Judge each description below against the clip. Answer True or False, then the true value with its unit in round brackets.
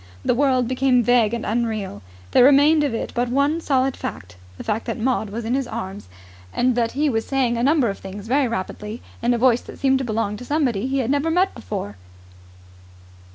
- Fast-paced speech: True (210 wpm)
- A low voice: False (245 Hz)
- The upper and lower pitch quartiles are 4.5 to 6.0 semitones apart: False (3.3 semitones)